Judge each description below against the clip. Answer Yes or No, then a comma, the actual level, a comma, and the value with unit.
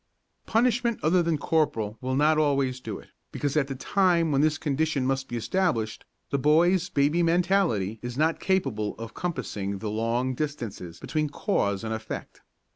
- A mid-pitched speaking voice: Yes, medium, 145 Hz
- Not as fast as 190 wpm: Yes, average, 165 wpm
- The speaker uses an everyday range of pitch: No, wide, 6.4 semitones